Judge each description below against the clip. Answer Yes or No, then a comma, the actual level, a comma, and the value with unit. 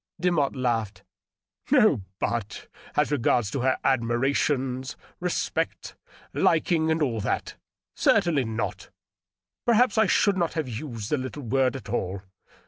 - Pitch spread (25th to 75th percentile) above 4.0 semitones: Yes, average, 5.2 semitones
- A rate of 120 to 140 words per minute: Yes, slow, 135 wpm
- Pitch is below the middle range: Yes, low, 130 Hz